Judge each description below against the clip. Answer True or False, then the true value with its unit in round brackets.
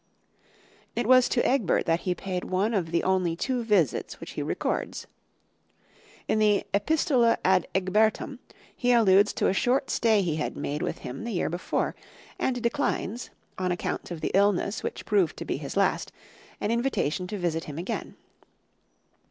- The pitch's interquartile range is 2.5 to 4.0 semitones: False (4.8 semitones)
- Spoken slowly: False (170 wpm)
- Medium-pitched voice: False (200 Hz)